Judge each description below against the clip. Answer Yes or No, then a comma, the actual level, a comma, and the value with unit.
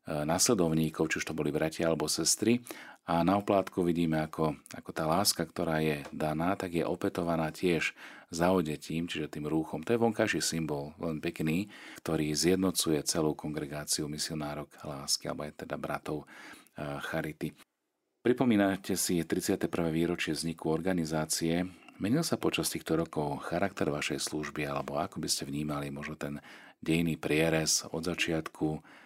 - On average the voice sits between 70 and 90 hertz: Yes, very low, 80 Hz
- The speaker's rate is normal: Yes, average, 140 wpm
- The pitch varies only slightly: Yes, narrow, 2.2 semitones